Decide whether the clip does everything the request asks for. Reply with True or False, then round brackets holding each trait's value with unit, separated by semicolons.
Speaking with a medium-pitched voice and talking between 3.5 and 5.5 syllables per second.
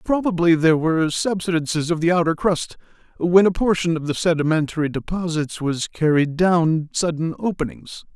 True (165 Hz; 5.2 syllables/s)